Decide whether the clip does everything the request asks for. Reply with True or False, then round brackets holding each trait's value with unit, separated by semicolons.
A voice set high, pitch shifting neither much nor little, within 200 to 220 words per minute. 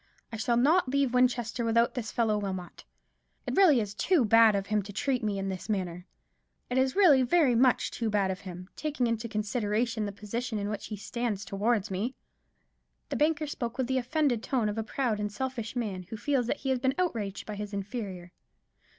True (230 Hz; 3.8 semitones; 205 wpm)